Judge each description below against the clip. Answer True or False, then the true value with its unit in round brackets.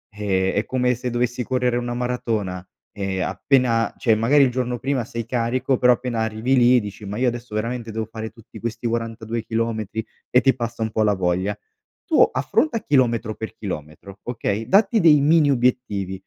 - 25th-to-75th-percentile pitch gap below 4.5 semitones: True (2.6 semitones)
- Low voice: True (115 Hz)